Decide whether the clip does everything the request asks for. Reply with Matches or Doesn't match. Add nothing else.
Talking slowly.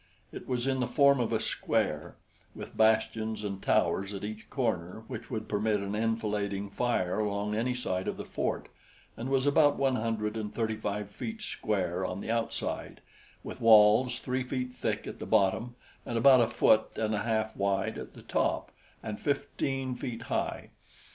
Doesn't match